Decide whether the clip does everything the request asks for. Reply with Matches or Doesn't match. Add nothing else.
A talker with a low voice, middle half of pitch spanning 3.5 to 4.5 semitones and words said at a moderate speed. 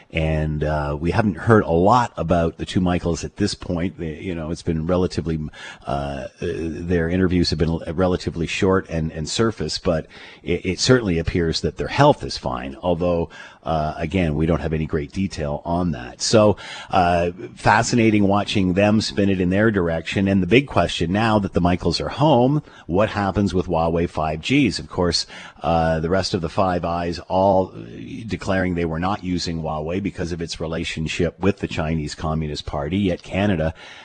Doesn't match